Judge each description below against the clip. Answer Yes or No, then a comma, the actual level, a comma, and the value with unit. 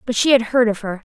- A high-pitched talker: Yes, high, 230 Hz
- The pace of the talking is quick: Yes, fast, 325 wpm